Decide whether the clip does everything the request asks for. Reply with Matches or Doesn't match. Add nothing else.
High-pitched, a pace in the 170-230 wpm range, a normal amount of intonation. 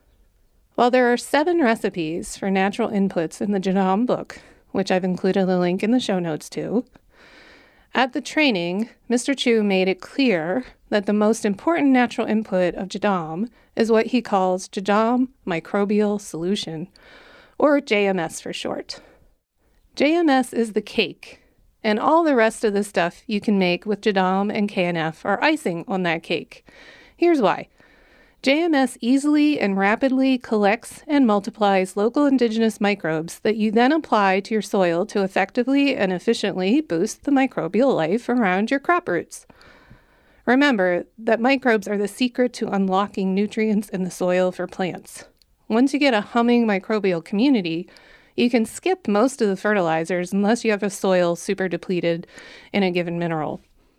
Doesn't match